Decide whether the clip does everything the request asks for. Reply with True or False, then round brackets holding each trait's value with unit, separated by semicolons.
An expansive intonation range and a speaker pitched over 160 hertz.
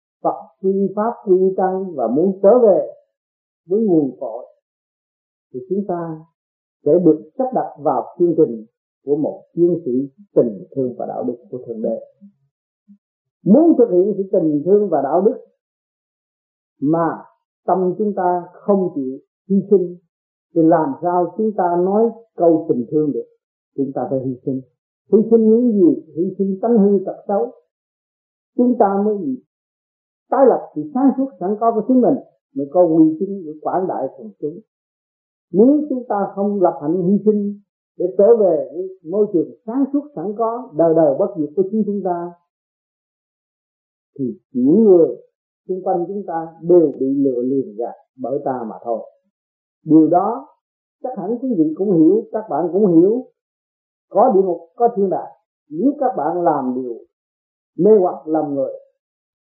True (6.1 semitones; 190 Hz)